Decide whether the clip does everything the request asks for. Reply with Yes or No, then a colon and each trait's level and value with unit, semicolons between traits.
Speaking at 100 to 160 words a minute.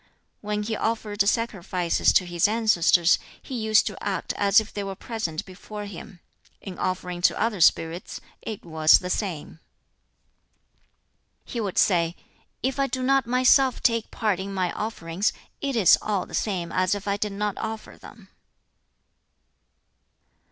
Yes: average, 150 wpm